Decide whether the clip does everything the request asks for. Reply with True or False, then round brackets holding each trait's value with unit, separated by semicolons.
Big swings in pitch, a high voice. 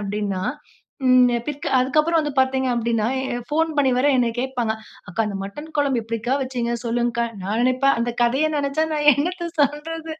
False (4.0 semitones; 255 Hz)